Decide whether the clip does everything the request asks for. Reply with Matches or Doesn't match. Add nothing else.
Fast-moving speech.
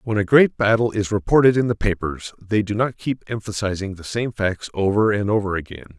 Matches